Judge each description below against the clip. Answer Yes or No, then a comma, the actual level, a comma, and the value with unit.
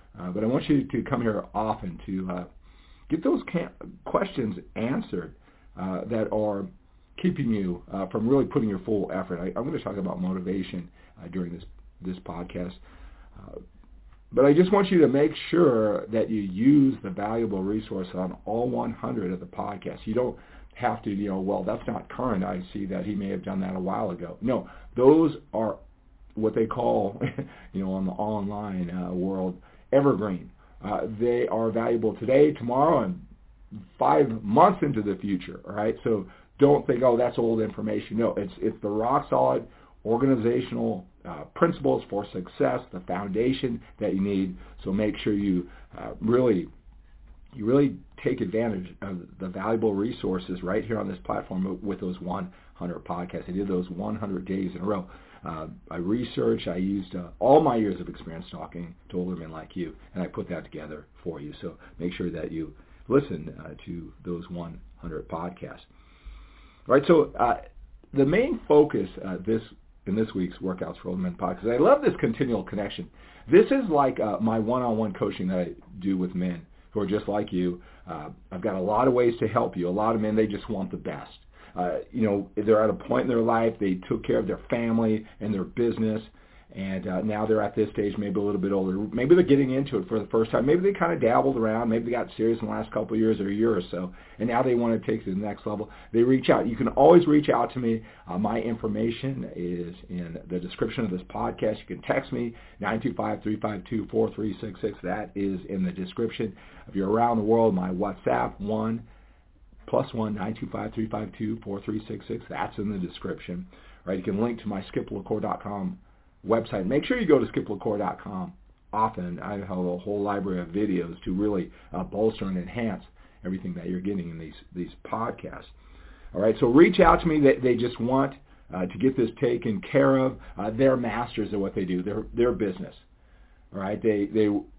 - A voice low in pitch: Yes, low, 105 Hz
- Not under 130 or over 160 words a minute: No, fast, 205 wpm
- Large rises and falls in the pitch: No, average, 3.7 semitones